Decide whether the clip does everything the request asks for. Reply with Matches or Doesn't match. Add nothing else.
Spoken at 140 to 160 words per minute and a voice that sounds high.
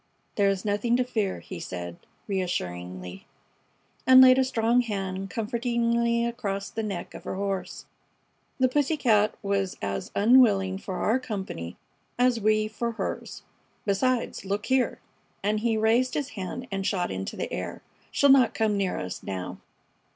Matches